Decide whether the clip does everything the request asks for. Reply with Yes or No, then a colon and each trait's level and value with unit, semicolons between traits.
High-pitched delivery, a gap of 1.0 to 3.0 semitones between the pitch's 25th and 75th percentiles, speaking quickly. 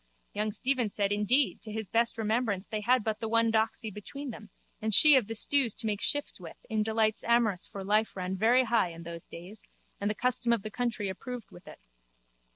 Yes: high, 220 Hz; narrow, 2.4 semitones; fast, 215 wpm